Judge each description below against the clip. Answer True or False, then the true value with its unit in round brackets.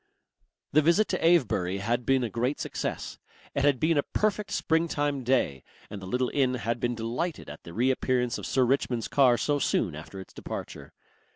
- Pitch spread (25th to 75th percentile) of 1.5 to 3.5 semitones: False (4.1 semitones)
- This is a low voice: True (130 Hz)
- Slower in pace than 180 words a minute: False (185 wpm)